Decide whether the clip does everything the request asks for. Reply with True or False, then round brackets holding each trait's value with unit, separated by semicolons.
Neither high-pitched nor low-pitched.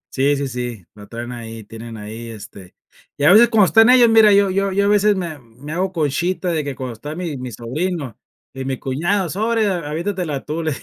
True (150 Hz)